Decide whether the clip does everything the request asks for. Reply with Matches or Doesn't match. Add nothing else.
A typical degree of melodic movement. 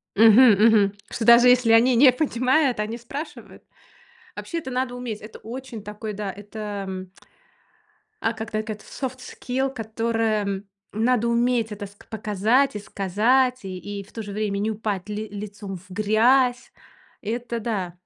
Matches